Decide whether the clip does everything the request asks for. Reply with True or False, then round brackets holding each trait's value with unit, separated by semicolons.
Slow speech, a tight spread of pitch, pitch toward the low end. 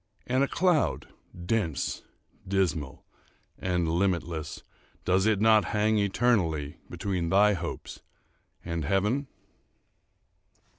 False (95 wpm; 4.4 semitones; 95 Hz)